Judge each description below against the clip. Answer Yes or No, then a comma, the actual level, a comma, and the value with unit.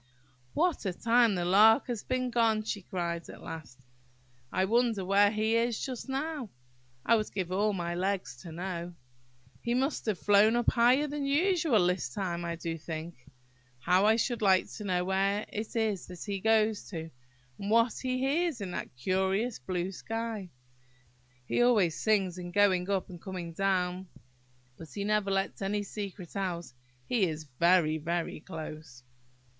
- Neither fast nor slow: Yes, average, 170 wpm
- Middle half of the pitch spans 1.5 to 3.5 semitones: No, average, 4.3 semitones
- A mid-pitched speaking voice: No, high, 195 Hz